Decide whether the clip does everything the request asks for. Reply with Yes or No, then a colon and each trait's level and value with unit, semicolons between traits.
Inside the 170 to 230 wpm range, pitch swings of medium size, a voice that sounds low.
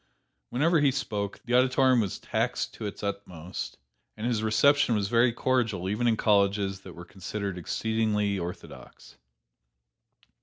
No: average, 140 wpm; average, 3.6 semitones; low, 105 Hz